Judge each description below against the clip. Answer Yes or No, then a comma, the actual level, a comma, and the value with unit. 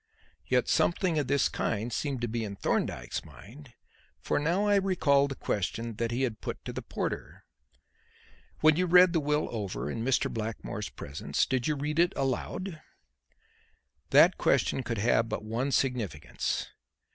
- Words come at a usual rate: Yes, average, 160 wpm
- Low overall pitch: Yes, low, 130 Hz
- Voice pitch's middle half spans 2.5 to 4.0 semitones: No, average, 5.2 semitones